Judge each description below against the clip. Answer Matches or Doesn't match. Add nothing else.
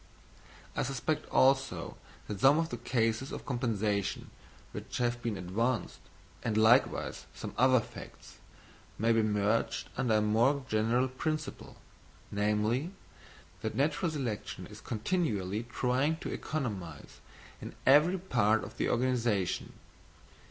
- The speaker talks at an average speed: Doesn't match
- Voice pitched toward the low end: Matches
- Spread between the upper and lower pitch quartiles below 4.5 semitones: Matches